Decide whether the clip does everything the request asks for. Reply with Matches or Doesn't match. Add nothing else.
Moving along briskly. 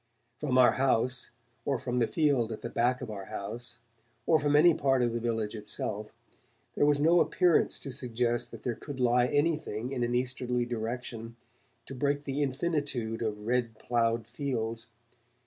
Doesn't match